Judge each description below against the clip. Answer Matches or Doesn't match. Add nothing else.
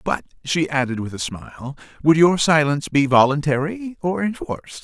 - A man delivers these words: Matches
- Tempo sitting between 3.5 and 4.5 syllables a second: Doesn't match